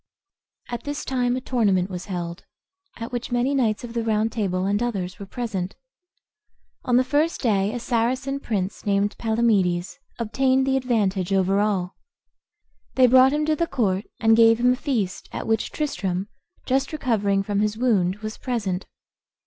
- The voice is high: Yes, high, 225 Hz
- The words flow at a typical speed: Yes, average, 165 wpm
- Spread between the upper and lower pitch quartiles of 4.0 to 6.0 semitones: Yes, average, 4.4 semitones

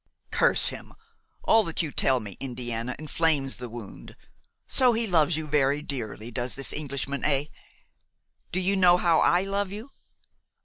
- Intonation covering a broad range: Yes, wide, 5.9 semitones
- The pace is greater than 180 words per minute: No, average, 160 wpm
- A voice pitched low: No, medium, 150 Hz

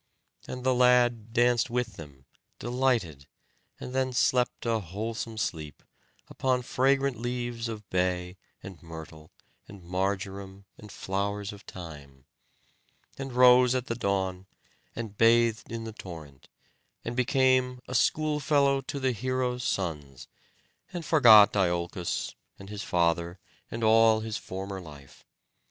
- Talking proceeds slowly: Yes, slow, 130 wpm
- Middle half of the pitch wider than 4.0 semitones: Yes, average, 5.3 semitones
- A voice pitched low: Yes, low, 110 Hz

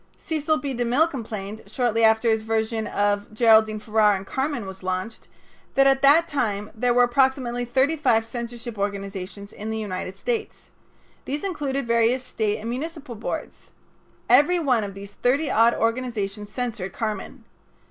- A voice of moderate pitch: No, high, 230 Hz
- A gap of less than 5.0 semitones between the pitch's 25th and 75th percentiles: Yes, average, 4.0 semitones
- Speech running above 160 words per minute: No, average, 155 wpm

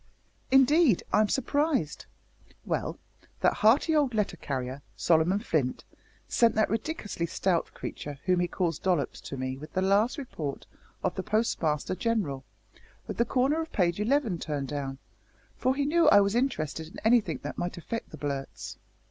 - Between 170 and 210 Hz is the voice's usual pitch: Yes, high, 190 Hz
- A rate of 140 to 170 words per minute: Yes, average, 160 wpm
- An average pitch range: No, wide, 7.8 semitones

